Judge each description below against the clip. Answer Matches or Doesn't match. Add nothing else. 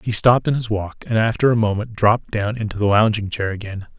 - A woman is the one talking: Doesn't match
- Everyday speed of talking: Doesn't match